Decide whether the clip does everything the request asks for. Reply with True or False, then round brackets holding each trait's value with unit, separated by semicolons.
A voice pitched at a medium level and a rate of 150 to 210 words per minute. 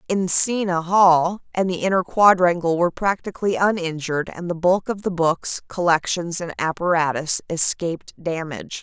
False (175 Hz; 135 wpm)